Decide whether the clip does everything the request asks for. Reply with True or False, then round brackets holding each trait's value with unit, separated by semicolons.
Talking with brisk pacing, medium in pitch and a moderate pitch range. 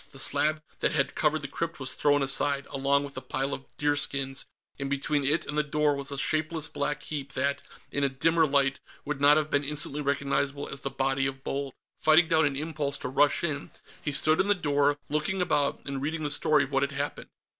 False (220 wpm; 145 Hz; 1.6 semitones)